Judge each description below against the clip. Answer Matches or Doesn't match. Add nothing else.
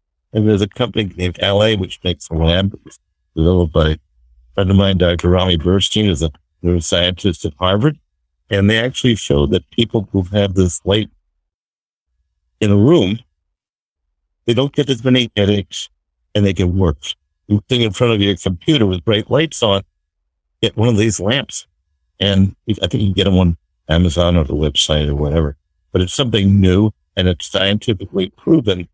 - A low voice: Matches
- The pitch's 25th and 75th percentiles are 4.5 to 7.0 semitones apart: Matches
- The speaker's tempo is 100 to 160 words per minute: Doesn't match